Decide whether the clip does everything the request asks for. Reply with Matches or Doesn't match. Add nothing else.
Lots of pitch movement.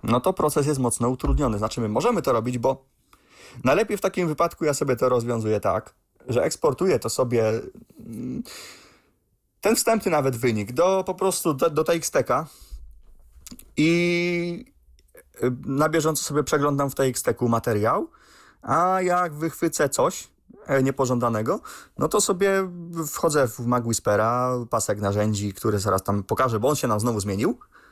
Matches